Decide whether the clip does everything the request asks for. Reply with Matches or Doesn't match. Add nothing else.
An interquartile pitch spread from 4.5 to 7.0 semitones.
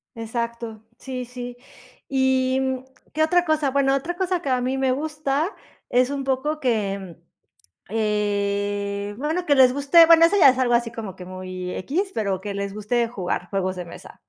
Matches